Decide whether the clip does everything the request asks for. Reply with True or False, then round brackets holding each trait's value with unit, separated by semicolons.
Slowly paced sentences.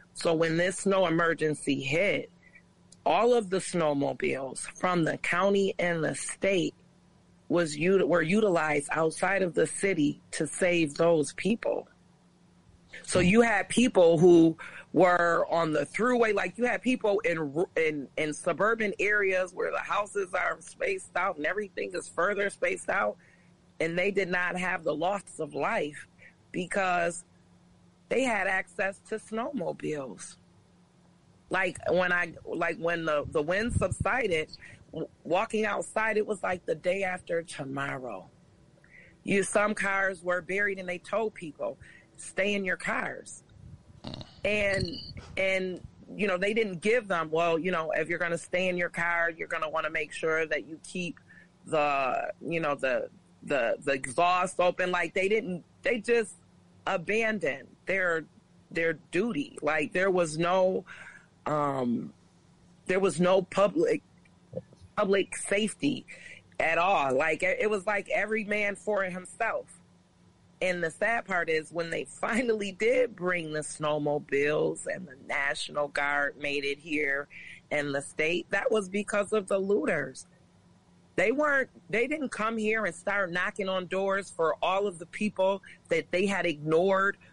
False (150 wpm)